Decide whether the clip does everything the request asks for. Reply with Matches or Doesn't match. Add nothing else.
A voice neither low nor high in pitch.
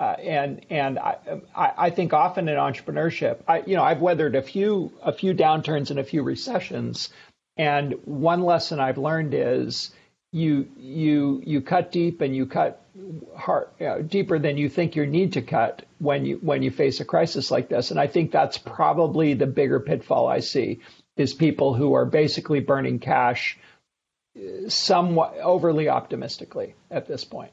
Matches